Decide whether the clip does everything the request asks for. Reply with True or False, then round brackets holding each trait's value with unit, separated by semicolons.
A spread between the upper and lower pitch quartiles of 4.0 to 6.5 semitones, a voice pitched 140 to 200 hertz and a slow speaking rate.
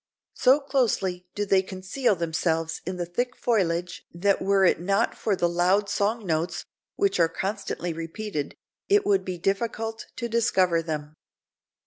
False (4.3 semitones; 190 Hz; 150 wpm)